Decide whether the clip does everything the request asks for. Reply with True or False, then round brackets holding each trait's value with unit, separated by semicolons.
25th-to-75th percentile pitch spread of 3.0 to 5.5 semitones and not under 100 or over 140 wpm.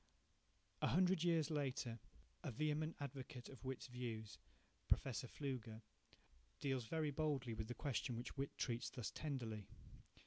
True (3.9 semitones; 135 wpm)